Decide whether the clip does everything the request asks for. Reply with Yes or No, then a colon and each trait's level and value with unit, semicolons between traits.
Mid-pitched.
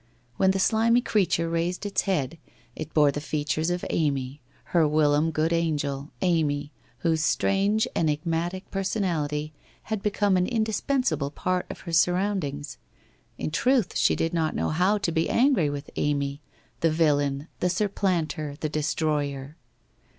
Yes: medium, 165 Hz